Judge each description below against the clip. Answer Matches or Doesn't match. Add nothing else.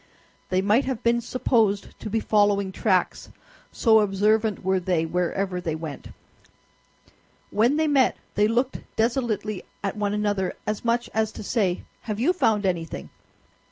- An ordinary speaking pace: Matches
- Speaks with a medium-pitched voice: Doesn't match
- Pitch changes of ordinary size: Matches